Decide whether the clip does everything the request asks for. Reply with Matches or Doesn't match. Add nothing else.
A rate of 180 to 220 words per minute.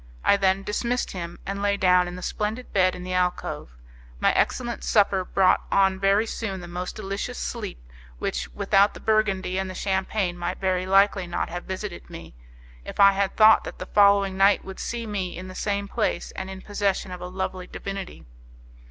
Matches